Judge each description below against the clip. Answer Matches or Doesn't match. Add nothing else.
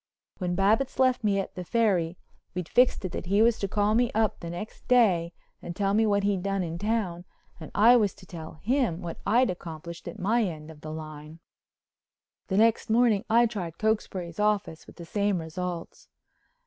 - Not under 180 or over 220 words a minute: Matches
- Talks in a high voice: Matches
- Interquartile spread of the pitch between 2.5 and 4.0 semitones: Doesn't match